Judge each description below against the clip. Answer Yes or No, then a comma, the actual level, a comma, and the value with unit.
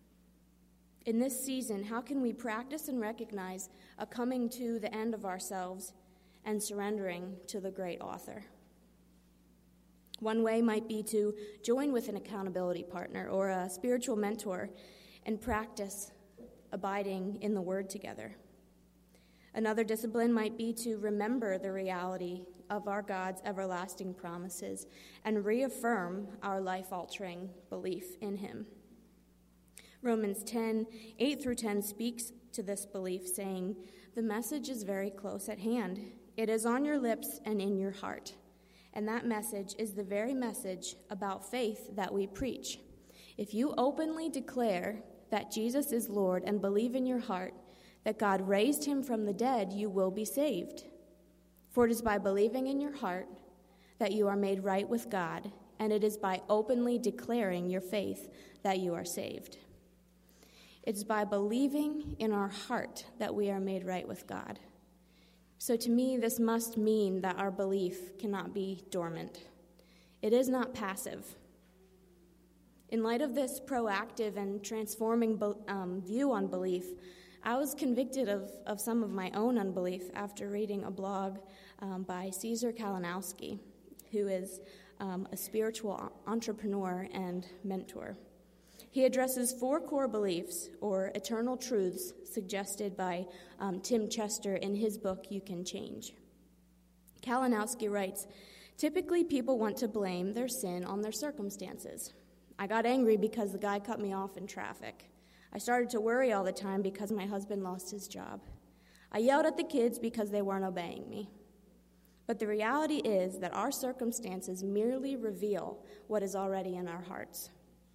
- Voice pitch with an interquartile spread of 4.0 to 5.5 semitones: No, average, 3.3 semitones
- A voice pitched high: Yes, high, 205 Hz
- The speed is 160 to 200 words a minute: No, average, 150 wpm